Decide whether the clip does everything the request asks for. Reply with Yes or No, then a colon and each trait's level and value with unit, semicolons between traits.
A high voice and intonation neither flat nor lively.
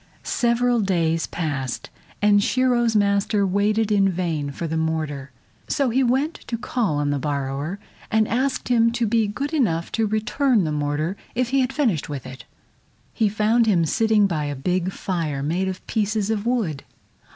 No: high, 200 Hz; wide, 6.4 semitones